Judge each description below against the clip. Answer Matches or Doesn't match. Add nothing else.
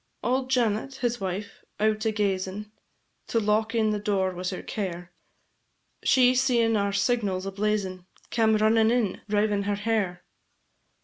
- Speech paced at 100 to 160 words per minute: Matches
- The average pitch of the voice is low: Doesn't match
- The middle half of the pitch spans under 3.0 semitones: Matches